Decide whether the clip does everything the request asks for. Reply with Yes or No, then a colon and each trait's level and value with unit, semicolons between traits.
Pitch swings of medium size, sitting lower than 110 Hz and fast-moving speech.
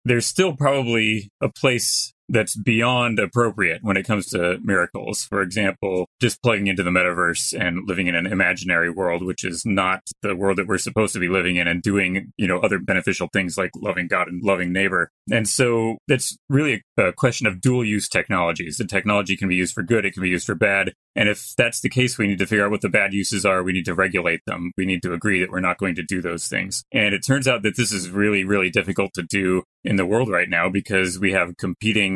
Yes: average, 3.2 semitones; low, 100 Hz; fast, 235 wpm